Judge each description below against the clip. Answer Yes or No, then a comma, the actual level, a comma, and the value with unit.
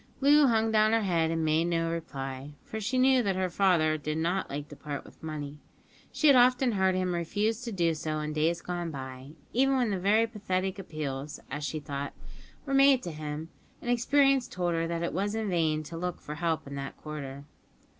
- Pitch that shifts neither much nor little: No, wide, 6.1 semitones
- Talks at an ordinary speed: No, fast, 210 wpm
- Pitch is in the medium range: Yes, medium, 170 Hz